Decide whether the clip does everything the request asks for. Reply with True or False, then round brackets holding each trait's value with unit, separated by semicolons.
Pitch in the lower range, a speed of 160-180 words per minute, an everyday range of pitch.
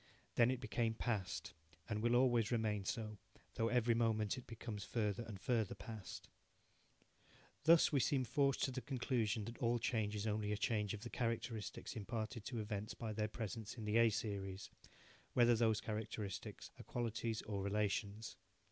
False (110 Hz; 165 wpm; 2.1 semitones)